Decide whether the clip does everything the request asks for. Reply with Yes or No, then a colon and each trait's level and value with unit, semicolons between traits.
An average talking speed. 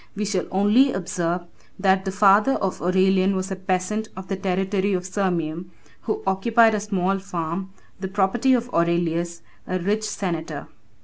Yes: average, 160 wpm